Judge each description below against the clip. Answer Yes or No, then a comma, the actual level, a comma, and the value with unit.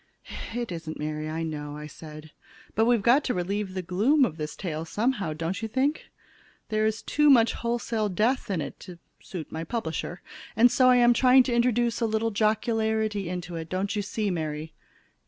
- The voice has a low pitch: No, high, 210 Hz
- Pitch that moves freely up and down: Yes, wide, 6.3 semitones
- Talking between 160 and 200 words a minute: Yes, average, 190 wpm